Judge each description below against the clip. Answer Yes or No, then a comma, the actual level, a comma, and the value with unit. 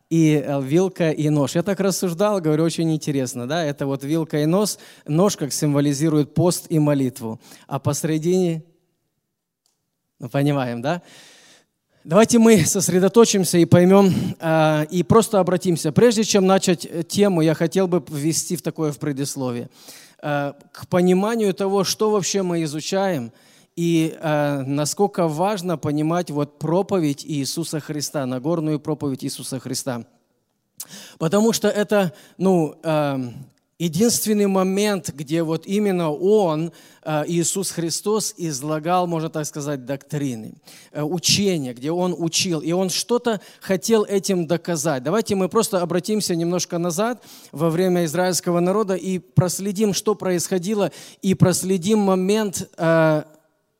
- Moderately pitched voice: Yes, medium, 170 Hz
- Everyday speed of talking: Yes, average, 130 wpm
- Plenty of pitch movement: No, average, 4.1 semitones